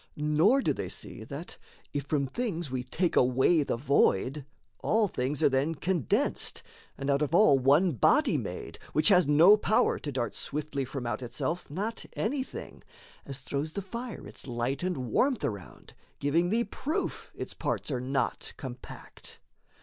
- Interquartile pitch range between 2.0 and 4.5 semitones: No, wide, 5.5 semitones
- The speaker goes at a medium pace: Yes, average, 165 wpm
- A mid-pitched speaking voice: Yes, medium, 150 Hz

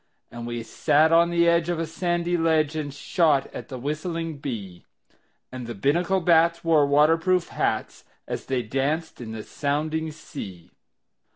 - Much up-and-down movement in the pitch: No, average, 3.8 semitones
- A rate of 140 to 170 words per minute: Yes, average, 165 wpm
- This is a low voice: No, medium, 155 Hz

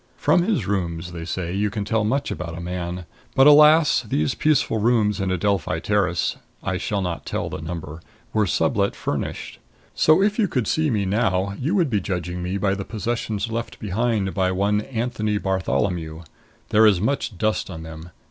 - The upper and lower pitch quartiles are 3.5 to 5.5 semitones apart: Yes, average, 4.4 semitones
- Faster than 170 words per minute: Yes, average, 185 wpm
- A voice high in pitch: No, low, 100 Hz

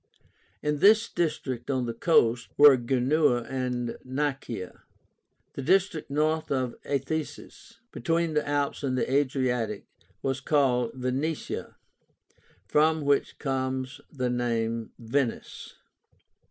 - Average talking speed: No, slow, 115 wpm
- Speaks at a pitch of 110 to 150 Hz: Yes, low, 135 Hz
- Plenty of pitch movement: No, average, 3.3 semitones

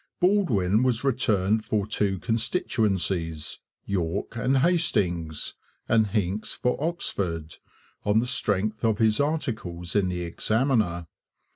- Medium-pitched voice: No, low, 105 Hz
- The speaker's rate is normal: No, slow, 115 wpm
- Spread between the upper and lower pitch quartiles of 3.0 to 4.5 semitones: No, average, 5.3 semitones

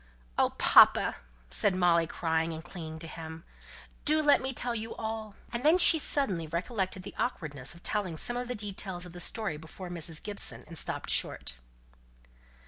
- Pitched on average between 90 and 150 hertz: No, medium, 180 Hz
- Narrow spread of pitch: No, wide, 5.6 semitones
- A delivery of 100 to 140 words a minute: No, average, 175 wpm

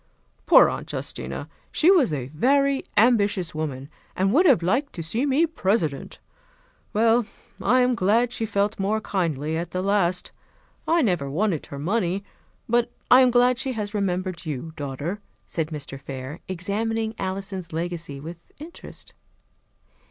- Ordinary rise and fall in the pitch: No, wide, 6.2 semitones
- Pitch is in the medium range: No, high, 195 Hz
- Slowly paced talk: No, average, 150 wpm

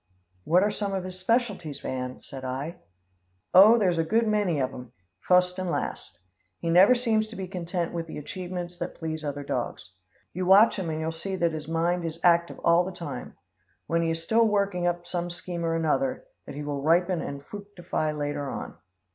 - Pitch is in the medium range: Yes, medium, 175 Hz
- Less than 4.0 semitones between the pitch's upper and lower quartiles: Yes, average, 3.2 semitones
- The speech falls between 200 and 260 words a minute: Yes, fast, 205 wpm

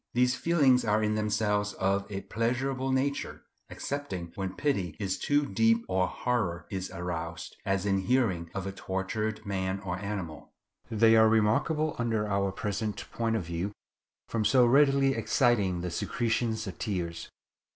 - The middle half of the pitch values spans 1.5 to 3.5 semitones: No, average, 4.0 semitones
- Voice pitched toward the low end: Yes, low, 105 Hz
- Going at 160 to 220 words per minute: No, average, 150 wpm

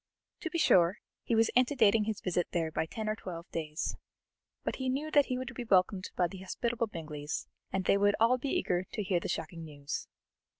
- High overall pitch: Yes, high, 200 Hz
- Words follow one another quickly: Yes, fast, 210 wpm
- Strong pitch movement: Yes, wide, 5.8 semitones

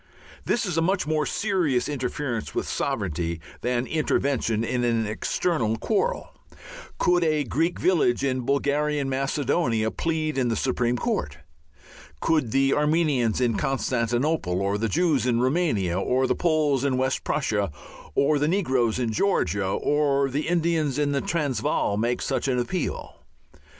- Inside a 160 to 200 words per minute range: No, average, 145 wpm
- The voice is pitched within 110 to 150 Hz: Yes, low, 135 Hz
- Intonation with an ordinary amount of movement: Yes, average, 4.6 semitones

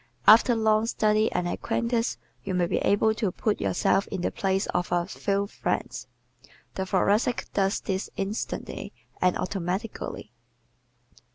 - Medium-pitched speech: No, high, 200 Hz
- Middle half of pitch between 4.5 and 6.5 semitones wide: No, narrow, 2.6 semitones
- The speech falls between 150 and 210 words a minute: No, average, 140 wpm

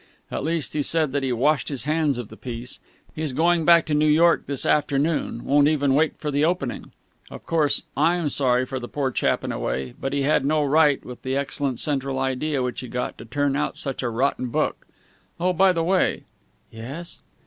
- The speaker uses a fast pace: Yes, fast, 215 wpm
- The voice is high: No, medium, 140 Hz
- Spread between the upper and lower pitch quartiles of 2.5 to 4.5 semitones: Yes, average, 3.1 semitones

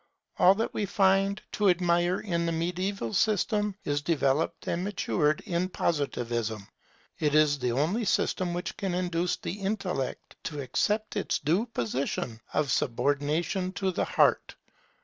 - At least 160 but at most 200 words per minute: No, average, 145 wpm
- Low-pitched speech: No, medium, 175 Hz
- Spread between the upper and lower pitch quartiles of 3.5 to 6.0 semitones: Yes, average, 5.1 semitones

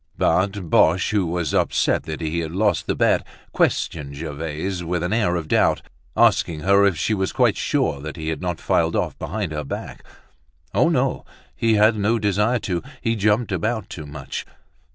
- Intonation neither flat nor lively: Yes, average, 4.5 semitones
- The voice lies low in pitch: Yes, very low, 90 Hz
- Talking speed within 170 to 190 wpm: Yes, average, 180 wpm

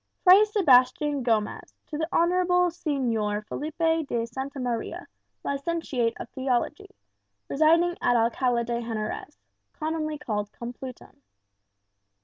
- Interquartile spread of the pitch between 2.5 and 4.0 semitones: No, wide, 5.6 semitones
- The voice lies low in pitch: No, very high, 275 Hz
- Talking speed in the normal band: No, slow, 110 wpm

